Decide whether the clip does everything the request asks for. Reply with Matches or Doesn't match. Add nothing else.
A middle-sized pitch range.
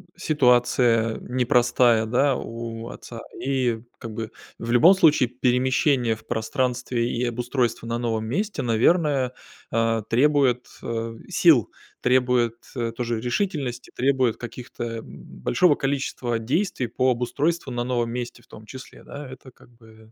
Doesn't match